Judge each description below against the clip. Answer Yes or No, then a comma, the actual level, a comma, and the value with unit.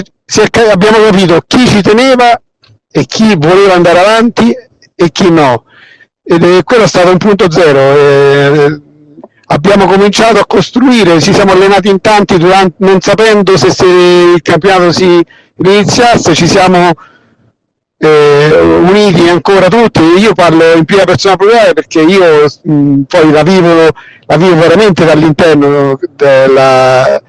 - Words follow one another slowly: No, average, 140 wpm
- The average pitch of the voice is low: No, medium, 180 Hz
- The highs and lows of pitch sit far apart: No, average, 4.3 semitones